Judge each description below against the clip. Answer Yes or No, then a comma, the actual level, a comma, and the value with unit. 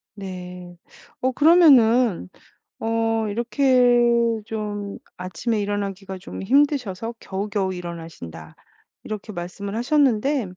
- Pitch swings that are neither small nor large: Yes, average, 4.4 semitones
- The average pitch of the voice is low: No, high, 210 Hz